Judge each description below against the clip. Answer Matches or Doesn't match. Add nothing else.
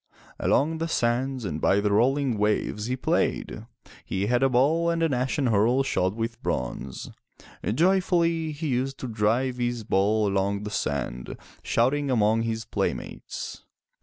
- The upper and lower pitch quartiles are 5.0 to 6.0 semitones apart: Doesn't match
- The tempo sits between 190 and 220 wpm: Doesn't match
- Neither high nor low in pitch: Doesn't match